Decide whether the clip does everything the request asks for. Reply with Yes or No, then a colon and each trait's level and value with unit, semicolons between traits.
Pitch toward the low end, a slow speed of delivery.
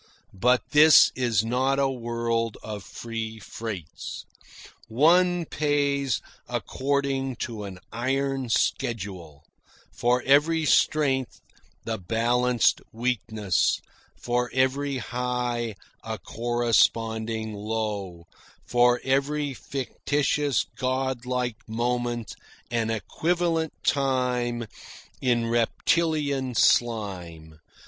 Yes: low, 120 Hz; slow, 85 wpm